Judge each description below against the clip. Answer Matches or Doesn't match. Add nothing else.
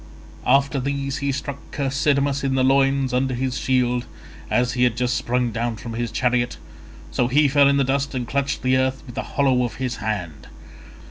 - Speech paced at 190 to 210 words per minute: Matches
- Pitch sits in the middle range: Doesn't match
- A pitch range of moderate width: Doesn't match